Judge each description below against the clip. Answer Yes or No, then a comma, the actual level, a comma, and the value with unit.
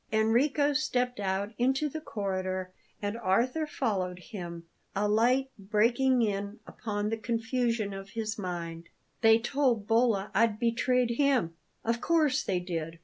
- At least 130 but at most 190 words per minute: Yes, average, 140 wpm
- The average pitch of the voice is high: Yes, high, 225 Hz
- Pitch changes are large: No, average, 4.2 semitones